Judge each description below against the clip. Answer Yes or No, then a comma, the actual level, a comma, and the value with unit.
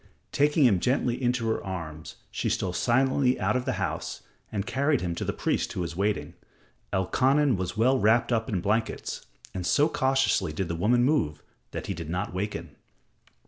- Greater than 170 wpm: Yes, average, 185 wpm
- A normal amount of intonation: No, wide, 6.3 semitones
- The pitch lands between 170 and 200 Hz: No, low, 110 Hz